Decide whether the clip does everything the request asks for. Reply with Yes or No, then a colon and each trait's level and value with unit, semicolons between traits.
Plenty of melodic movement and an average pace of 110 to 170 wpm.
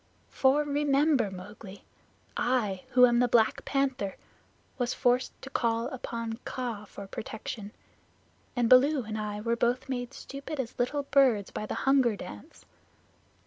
No: average, 3.7 semitones; average, 145 wpm